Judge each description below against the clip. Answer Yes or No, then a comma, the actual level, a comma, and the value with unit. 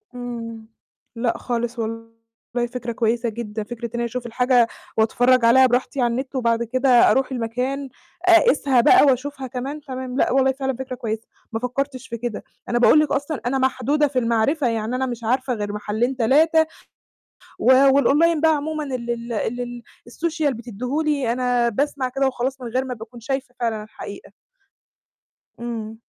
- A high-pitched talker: Yes, very high, 250 Hz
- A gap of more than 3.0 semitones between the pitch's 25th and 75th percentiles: No, narrow, 2.4 semitones